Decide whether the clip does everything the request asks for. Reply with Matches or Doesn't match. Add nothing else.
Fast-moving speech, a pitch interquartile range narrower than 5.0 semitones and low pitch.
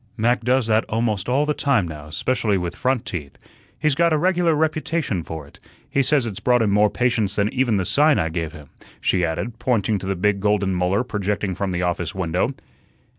Doesn't match